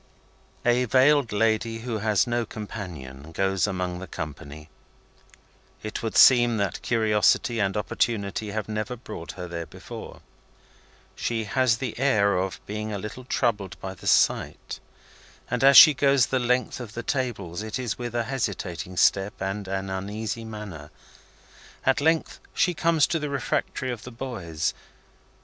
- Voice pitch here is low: Yes, low, 110 Hz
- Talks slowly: No, average, 155 wpm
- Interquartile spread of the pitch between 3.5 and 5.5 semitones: Yes, average, 4.3 semitones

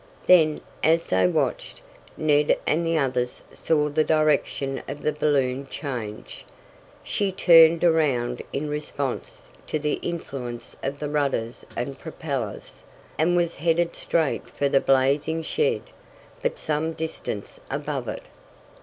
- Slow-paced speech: Yes, slow, 130 wpm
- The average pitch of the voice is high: No, medium, 150 Hz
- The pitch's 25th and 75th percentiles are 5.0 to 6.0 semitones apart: No, average, 3.1 semitones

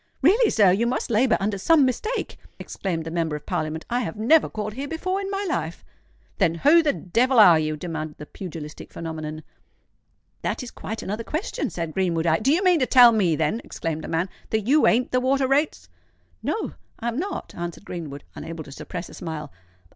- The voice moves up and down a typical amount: No, wide, 8.5 semitones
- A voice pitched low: No, high, 210 Hz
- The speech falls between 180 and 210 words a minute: Yes, average, 195 wpm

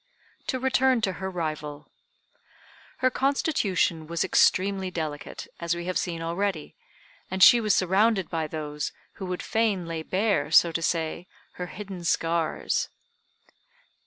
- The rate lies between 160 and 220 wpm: No, slow, 135 wpm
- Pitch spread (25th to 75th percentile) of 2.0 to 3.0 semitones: No, average, 3.5 semitones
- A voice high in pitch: No, medium, 180 Hz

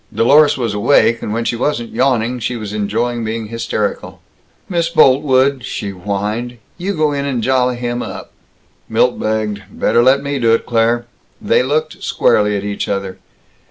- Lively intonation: No, average, 3.4 semitones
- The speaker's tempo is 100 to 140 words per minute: No, average, 165 wpm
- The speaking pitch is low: Yes, low, 120 Hz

